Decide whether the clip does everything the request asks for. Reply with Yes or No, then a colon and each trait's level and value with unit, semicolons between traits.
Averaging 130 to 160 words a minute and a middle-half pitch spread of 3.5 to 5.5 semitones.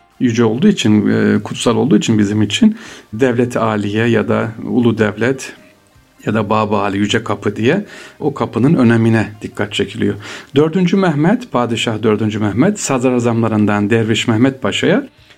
No: average, 135 wpm; average, 2.8 semitones